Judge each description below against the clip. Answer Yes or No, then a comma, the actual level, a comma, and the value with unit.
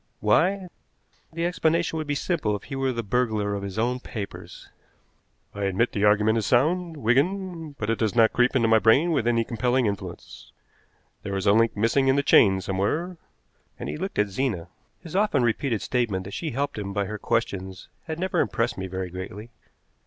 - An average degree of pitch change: No, wide, 6.1 semitones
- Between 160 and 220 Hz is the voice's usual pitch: No, low, 115 Hz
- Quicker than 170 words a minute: Yes, average, 195 wpm